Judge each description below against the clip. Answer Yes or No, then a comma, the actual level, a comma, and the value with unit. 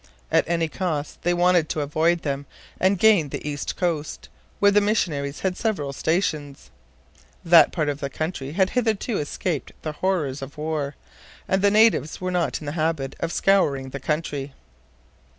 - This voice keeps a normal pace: Yes, average, 170 wpm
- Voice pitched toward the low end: No, medium, 160 Hz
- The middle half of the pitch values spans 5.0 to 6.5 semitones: No, average, 4.3 semitones